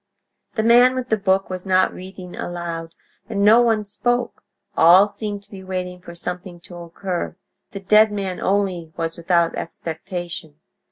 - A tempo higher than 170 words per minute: No, average, 160 wpm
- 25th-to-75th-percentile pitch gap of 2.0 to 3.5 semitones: Yes, average, 2.9 semitones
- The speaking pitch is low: No, medium, 185 Hz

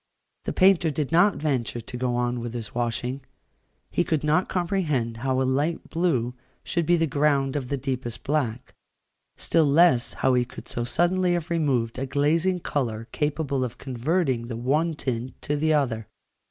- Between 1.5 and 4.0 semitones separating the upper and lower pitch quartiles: No, average, 4.8 semitones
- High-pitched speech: No, medium, 140 Hz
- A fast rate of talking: No, average, 175 wpm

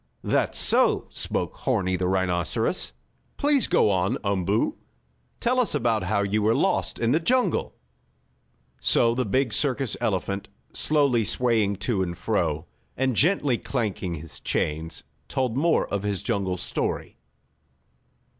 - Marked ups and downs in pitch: Yes, wide, 5.8 semitones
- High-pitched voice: No, low, 110 Hz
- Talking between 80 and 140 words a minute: Yes, slow, 135 wpm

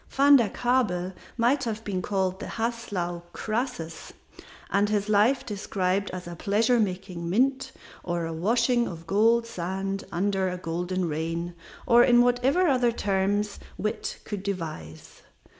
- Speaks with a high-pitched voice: Yes, high, 200 Hz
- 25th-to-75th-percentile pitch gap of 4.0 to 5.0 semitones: Yes, average, 4.6 semitones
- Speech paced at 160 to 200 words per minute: No, average, 140 wpm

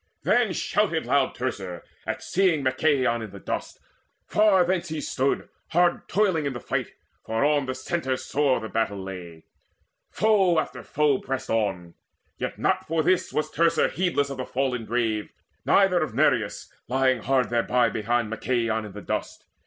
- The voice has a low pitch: Yes, low, 130 Hz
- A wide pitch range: Yes, wide, 6.1 semitones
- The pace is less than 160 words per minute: No, average, 165 wpm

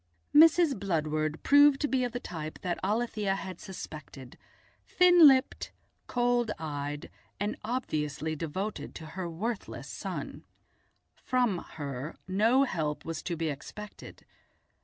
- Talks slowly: Yes, slow, 125 wpm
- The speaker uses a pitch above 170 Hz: Yes, high, 190 Hz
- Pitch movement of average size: No, wide, 7.8 semitones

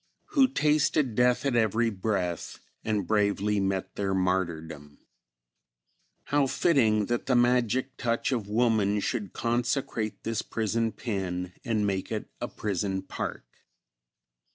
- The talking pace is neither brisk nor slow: No, slow, 125 wpm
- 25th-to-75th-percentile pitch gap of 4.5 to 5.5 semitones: No, average, 3.9 semitones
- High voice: No, low, 110 Hz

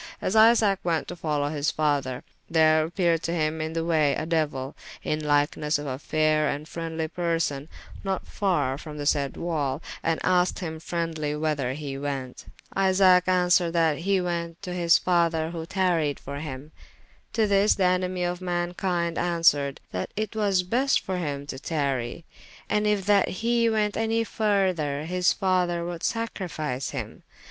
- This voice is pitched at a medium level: Yes, medium, 165 Hz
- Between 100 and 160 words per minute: No, average, 170 wpm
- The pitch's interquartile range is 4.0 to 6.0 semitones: No, average, 3.5 semitones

